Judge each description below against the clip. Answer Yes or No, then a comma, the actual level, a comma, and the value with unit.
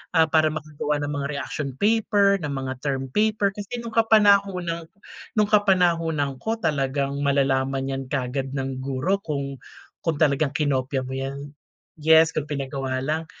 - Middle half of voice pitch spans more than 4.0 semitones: Yes, average, 4.6 semitones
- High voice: No, medium, 145 Hz